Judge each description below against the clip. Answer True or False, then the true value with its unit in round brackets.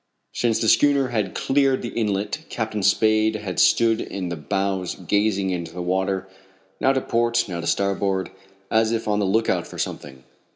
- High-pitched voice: False (105 Hz)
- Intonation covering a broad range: False (3.2 semitones)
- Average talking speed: True (175 wpm)